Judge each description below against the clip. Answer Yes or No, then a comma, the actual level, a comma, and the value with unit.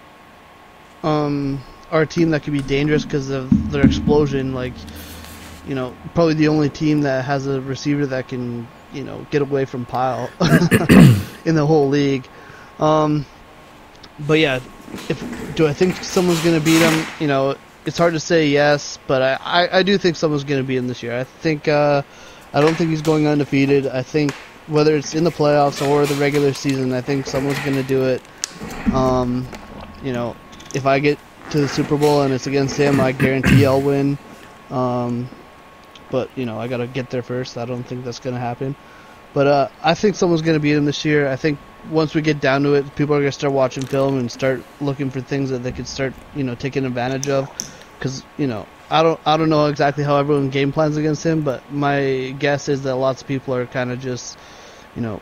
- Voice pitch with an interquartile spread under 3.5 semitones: Yes, narrow, 2.5 semitones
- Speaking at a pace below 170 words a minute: No, fast, 205 wpm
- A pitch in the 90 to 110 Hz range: No, medium, 140 Hz